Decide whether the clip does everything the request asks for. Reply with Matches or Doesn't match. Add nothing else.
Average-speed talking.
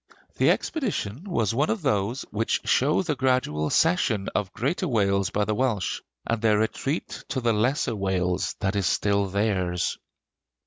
Matches